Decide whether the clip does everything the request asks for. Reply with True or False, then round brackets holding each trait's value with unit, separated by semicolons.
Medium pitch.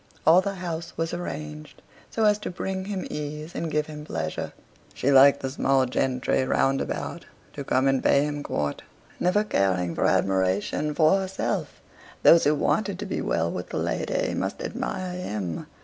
True (150 Hz)